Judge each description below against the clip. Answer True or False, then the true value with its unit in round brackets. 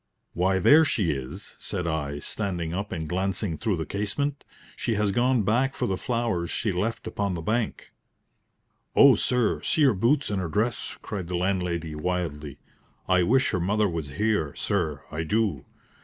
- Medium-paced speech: True (170 wpm)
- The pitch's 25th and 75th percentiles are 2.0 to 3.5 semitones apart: False (4.8 semitones)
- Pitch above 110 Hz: False (95 Hz)